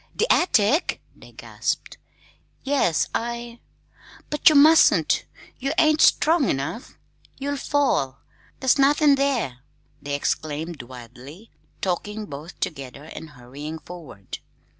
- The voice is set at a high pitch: Yes, high, 205 Hz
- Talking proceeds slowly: Yes, slow, 115 wpm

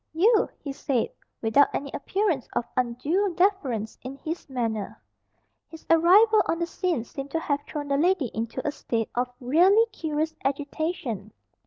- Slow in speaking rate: No, average, 155 wpm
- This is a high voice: Yes, very high, 290 Hz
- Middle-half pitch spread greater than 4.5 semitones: Yes, wide, 5.6 semitones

